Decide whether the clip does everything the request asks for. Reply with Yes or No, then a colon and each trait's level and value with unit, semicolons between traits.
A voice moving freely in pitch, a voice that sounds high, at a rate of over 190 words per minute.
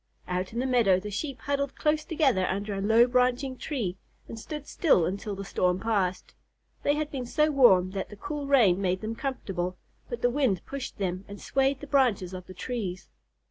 Yes: wide, 6.5 semitones; high, 225 Hz; average, 200 wpm